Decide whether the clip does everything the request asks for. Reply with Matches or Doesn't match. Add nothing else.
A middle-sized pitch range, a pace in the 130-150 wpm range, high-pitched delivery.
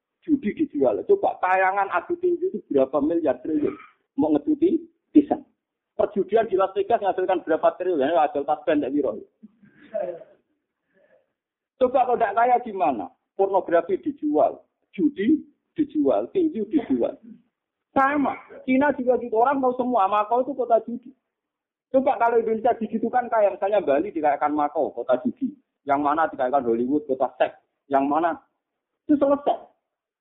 Doesn't match